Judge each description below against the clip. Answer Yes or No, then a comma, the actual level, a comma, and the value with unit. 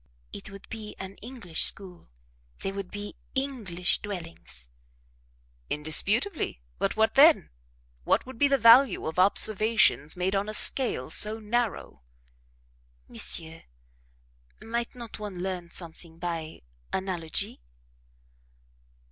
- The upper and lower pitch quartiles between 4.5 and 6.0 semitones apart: Yes, average, 4.8 semitones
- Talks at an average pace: No, slow, 115 wpm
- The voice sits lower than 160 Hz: No, high, 195 Hz